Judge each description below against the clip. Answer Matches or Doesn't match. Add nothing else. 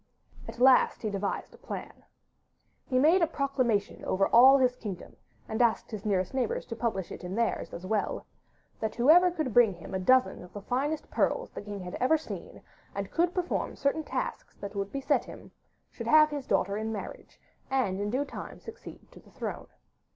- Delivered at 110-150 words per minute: Doesn't match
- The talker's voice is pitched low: Doesn't match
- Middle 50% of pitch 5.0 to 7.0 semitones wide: Matches